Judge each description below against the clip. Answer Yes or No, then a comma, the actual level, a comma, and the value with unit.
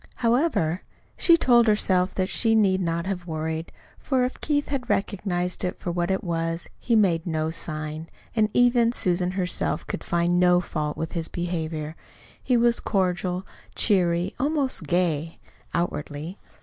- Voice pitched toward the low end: No, medium, 180 Hz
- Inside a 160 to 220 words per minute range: No, average, 150 wpm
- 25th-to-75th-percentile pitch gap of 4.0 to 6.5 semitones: Yes, average, 4.6 semitones